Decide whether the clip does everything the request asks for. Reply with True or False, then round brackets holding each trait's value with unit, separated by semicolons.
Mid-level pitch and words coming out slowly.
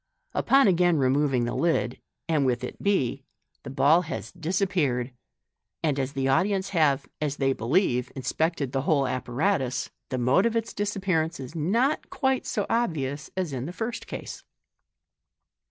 False (150 Hz; 160 wpm)